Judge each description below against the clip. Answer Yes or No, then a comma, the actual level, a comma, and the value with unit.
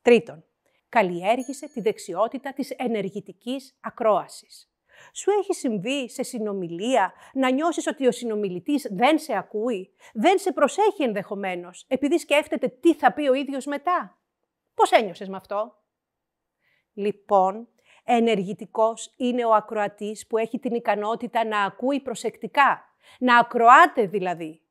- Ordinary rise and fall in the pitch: Yes, average, 4.5 semitones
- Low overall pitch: No, high, 235 Hz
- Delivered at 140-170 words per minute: No, average, 125 wpm